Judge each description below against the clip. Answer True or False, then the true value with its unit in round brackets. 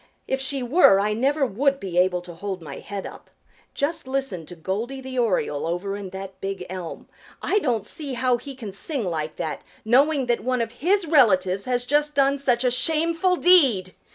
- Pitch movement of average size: False (6.4 semitones)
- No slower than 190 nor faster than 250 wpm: True (195 wpm)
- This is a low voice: False (245 Hz)